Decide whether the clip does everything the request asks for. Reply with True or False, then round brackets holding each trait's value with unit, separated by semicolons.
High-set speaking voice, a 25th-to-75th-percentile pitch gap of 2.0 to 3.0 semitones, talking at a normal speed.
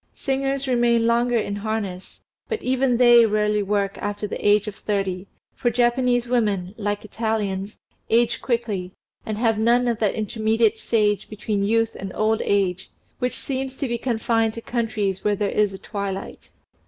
True (220 Hz; 2.7 semitones; 165 wpm)